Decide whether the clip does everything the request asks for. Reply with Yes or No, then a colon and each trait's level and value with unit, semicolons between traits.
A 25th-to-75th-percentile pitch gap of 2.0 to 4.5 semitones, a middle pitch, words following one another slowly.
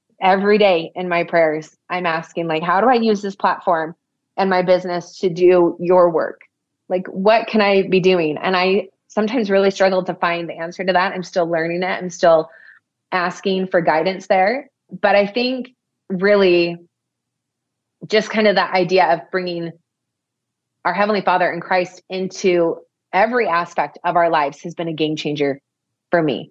No: narrow, 2.4 semitones; medium, 180 Hz; average, 175 wpm